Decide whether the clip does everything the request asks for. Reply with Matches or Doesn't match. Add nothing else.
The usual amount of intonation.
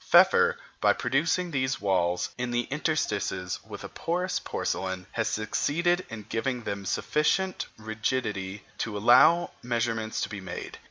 Doesn't match